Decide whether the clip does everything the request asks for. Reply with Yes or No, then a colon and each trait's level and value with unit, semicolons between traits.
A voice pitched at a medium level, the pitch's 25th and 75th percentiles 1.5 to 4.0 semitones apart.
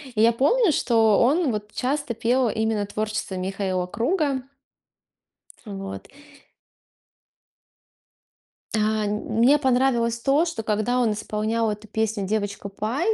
No: high, 225 Hz; average, 3.3 semitones